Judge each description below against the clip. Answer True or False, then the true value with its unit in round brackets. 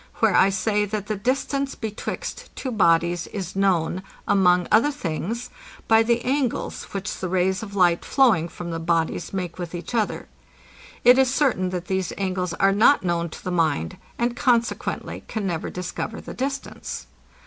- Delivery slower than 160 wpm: False (170 wpm)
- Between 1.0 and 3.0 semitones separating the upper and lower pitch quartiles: False (4.9 semitones)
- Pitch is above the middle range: True (195 Hz)